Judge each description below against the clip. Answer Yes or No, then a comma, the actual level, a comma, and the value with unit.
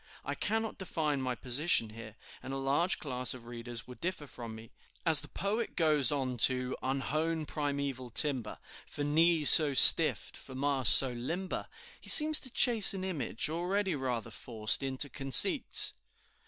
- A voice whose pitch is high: No, medium, 140 Hz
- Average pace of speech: Yes, average, 160 wpm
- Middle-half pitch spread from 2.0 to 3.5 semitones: No, average, 4.7 semitones